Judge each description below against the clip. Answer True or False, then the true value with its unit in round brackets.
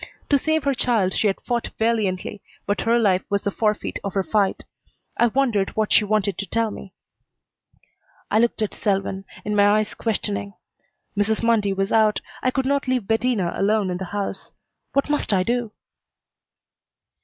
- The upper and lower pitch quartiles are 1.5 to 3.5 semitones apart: True (3.0 semitones)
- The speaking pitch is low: False (210 Hz)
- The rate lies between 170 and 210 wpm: True (175 wpm)